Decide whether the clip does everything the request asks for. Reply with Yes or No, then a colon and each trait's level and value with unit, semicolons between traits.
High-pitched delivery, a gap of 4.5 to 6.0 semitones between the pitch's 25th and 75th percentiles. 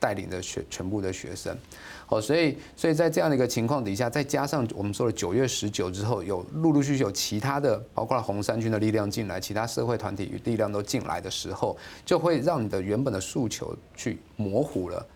No: low, 115 Hz; average, 5.3 semitones